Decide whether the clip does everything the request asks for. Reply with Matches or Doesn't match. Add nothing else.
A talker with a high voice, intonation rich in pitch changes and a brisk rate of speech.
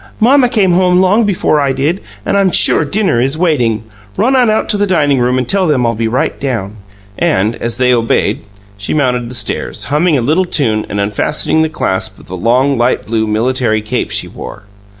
Doesn't match